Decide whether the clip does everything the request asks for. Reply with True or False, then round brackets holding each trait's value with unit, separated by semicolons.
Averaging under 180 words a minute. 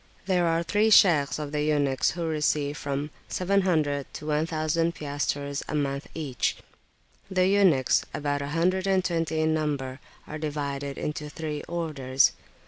True (145 wpm)